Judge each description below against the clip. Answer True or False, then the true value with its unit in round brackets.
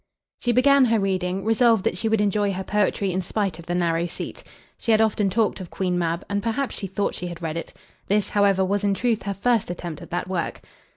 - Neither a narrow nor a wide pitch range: True (3.4 semitones)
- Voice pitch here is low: False (195 Hz)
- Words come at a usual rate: False (235 wpm)